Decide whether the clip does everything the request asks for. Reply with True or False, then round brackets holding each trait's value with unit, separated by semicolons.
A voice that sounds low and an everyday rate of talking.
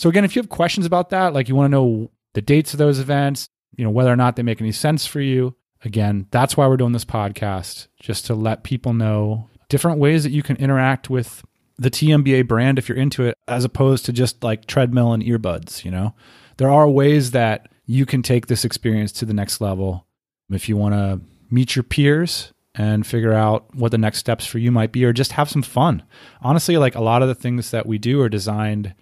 False (125 Hz; 235 wpm)